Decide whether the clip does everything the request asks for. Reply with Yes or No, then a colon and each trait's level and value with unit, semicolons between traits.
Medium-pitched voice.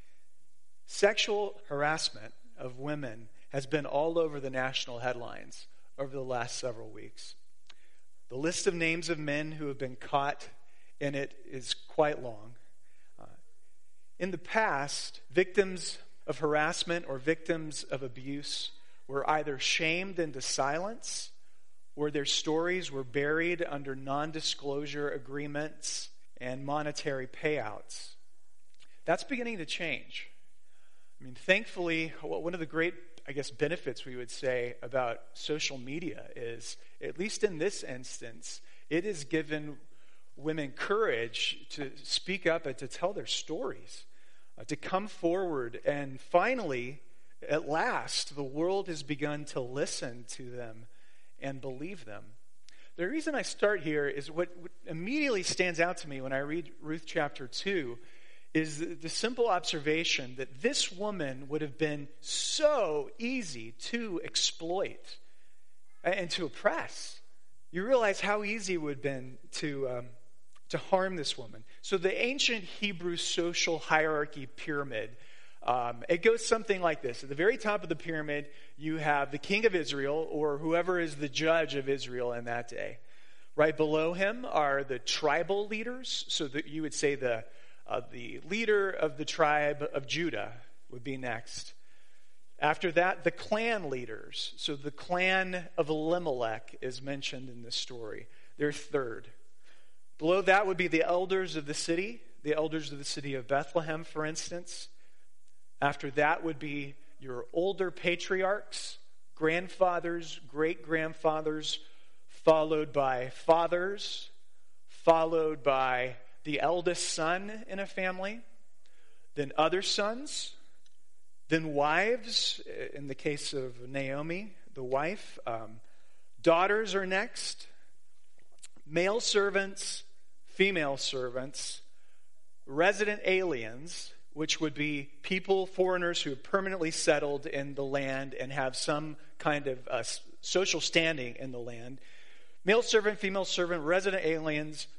Yes: medium, 155 Hz